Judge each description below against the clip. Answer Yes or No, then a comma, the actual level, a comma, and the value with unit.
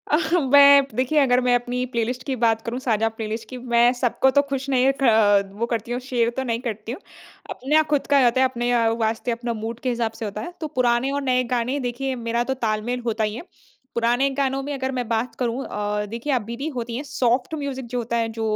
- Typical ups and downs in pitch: No, narrow, 2.3 semitones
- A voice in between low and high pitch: No, high, 245 Hz